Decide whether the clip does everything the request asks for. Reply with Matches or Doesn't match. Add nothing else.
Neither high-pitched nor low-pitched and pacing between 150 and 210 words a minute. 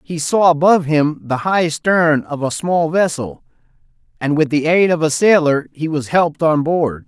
Matches